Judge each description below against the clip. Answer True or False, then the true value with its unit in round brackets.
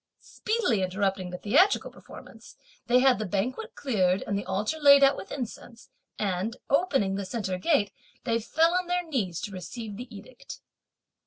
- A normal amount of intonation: False (6.3 semitones)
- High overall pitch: True (230 Hz)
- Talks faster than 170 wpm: False (165 wpm)